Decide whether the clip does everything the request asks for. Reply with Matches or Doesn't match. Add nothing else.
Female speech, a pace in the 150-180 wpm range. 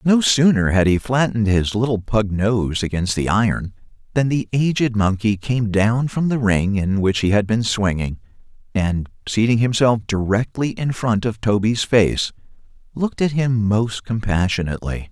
Doesn't match